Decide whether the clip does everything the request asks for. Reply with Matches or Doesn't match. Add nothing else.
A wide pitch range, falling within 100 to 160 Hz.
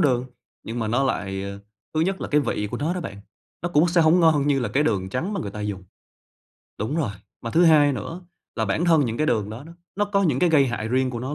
Matches